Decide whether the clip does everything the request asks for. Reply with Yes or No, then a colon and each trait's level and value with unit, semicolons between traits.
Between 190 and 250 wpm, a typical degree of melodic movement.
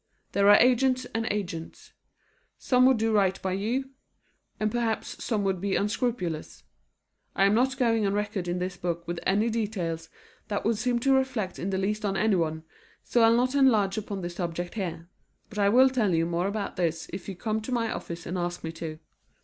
Yes: average, 200 wpm; average, 4.3 semitones